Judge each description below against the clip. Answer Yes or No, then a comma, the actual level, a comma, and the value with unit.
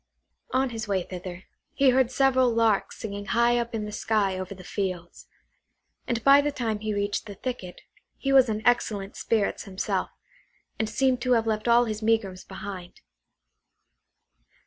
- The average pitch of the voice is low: No, high, 220 Hz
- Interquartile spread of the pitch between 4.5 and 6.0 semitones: No, average, 3.5 semitones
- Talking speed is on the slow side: No, average, 165 wpm